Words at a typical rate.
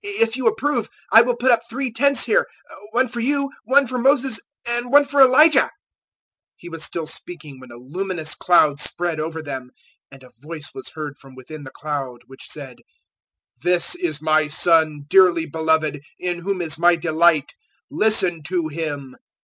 Yes: average, 175 wpm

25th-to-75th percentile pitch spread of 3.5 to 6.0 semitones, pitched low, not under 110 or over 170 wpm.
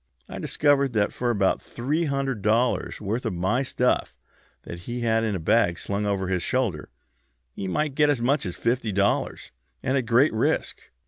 No: average, 4.9 semitones; low, 115 Hz; average, 185 wpm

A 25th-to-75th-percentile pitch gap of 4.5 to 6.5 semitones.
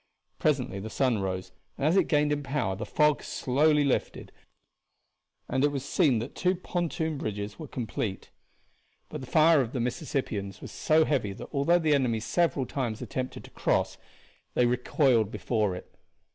Yes: average, 5.2 semitones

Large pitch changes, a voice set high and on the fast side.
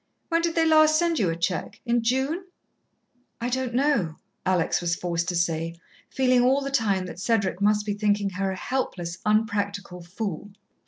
No: wide, 6.3 semitones; high, 205 Hz; average, 175 wpm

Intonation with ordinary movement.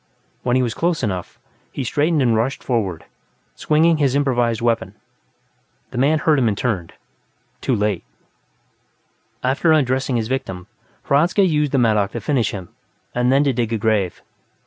Yes: average, 4.5 semitones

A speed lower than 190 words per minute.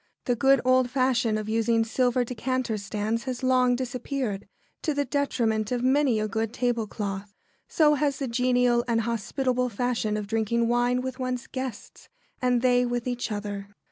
Yes: average, 165 wpm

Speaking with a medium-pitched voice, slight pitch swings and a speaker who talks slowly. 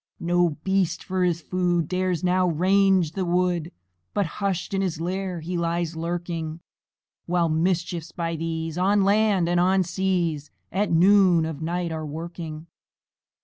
No: medium, 175 Hz; narrow, 2.1 semitones; average, 150 wpm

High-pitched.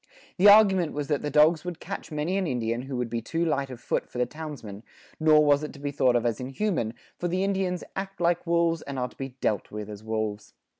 No: medium, 150 Hz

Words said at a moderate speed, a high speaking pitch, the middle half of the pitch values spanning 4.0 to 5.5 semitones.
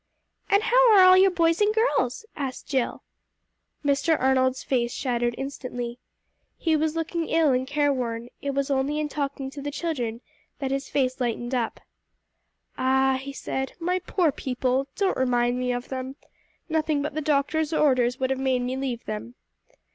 No: average, 170 wpm; very high, 270 Hz; average, 3.5 semitones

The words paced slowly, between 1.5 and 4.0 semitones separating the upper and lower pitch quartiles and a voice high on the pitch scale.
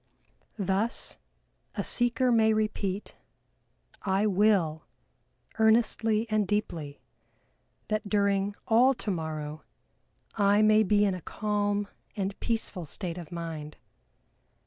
Yes: slow, 100 wpm; average, 2.9 semitones; high, 205 Hz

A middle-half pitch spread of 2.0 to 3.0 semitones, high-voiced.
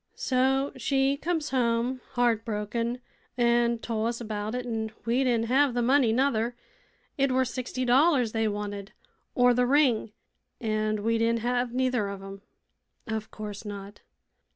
Yes: average, 2.7 semitones; high, 235 Hz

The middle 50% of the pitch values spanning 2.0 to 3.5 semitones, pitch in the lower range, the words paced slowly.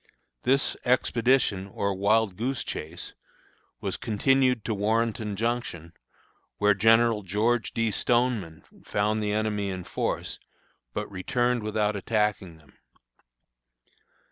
Yes: average, 2.9 semitones; low, 105 Hz; slow, 110 wpm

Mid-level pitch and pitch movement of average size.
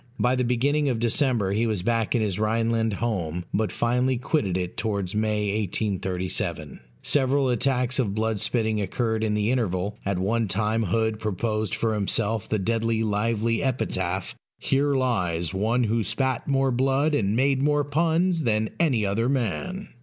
No: low, 115 Hz; average, 3.7 semitones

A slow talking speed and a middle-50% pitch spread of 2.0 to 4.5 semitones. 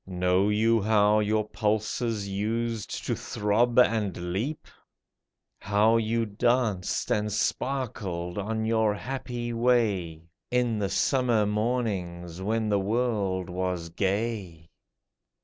Yes: slow, 110 wpm; average, 3.1 semitones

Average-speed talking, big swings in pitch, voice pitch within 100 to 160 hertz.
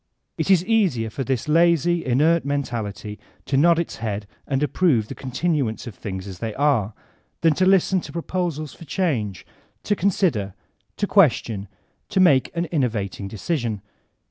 Yes: average, 160 wpm; wide, 7.5 semitones; medium, 140 Hz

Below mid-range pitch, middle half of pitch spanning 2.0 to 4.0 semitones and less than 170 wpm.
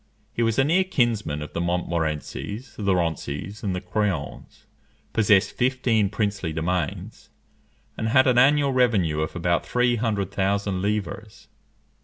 No: low, 100 Hz; average, 5.2 semitones; average, 140 wpm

